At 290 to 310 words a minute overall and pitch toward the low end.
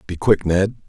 No: fast, 205 wpm; low, 100 Hz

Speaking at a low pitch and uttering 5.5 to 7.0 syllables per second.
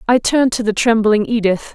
No: high, 225 Hz; 5.7 syllables/s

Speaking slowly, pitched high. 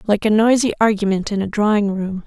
No: fast, 210 wpm; high, 210 Hz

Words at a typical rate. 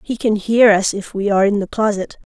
No: fast, 255 wpm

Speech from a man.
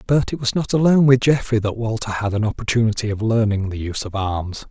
Yes: male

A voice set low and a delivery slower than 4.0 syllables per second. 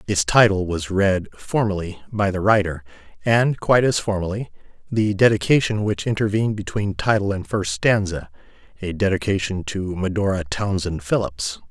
No: low, 100 Hz; 5.0 syllables/s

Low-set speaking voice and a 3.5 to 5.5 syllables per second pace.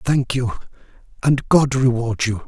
Yes: low, 125 Hz; 4.2 syllables/s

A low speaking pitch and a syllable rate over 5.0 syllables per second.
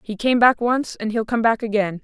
No: high, 225 Hz; 5.2 syllables/s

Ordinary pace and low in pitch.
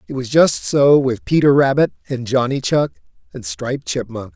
Yes: average, 180 wpm; low, 125 Hz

